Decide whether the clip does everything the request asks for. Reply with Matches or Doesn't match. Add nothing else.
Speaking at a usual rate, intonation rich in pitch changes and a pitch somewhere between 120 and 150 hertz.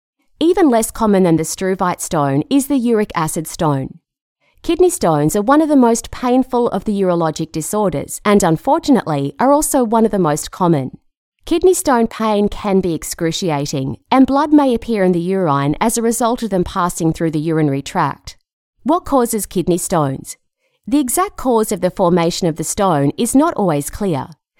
Doesn't match